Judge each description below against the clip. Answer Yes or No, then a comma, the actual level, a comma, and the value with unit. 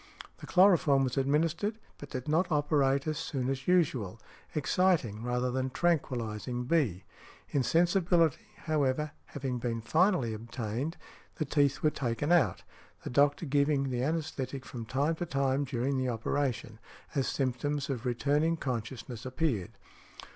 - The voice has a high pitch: No, low, 135 Hz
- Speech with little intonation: No, average, 3.9 semitones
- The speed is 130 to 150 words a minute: Yes, slow, 135 wpm